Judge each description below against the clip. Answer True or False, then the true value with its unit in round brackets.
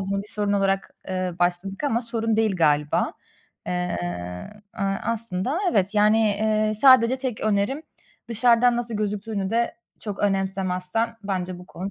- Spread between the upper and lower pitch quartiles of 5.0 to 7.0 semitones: False (3.1 semitones)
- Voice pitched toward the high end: True (205 Hz)